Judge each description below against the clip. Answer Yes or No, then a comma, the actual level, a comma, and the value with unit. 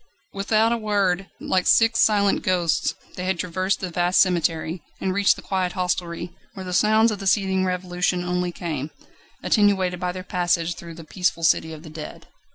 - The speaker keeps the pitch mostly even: Yes, narrow, 2.0 semitones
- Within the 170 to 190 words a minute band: Yes, average, 180 wpm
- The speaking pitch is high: No, medium, 180 Hz